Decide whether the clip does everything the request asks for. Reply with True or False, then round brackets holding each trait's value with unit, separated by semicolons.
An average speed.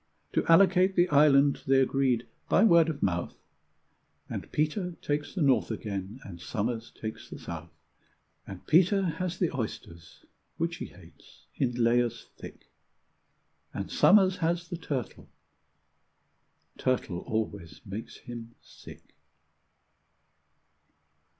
False (120 wpm)